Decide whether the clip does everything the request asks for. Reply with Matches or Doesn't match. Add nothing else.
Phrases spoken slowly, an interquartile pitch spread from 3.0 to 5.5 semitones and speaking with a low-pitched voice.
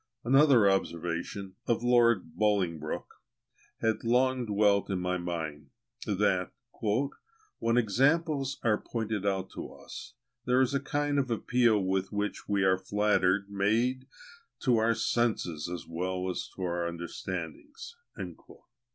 Matches